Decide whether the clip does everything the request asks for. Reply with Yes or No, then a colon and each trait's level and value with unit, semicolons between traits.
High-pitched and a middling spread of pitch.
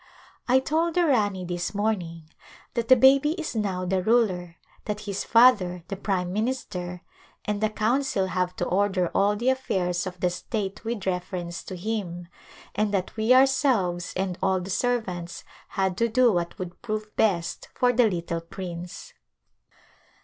Yes: high, 195 Hz; average, 4.4 semitones